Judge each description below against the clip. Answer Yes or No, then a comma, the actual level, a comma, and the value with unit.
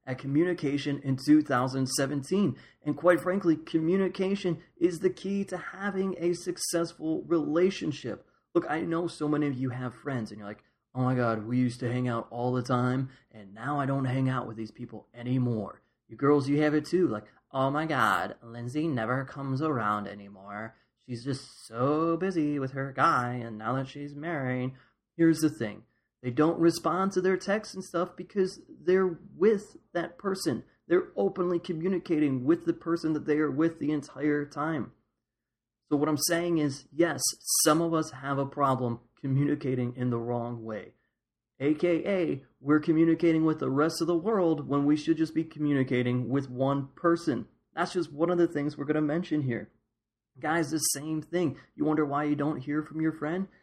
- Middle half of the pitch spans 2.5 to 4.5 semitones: No, average, 4.9 semitones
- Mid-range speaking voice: Yes, medium, 150 Hz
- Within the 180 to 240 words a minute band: Yes, average, 185 wpm